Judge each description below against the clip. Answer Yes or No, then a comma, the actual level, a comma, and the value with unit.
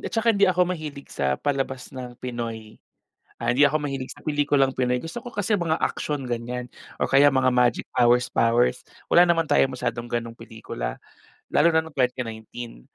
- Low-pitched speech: Yes, low, 130 Hz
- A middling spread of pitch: Yes, average, 4.1 semitones